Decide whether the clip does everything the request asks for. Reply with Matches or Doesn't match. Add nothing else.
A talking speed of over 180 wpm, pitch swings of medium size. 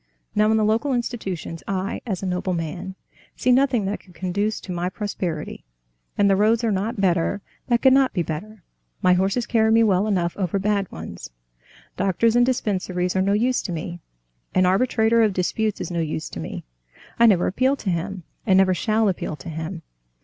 Matches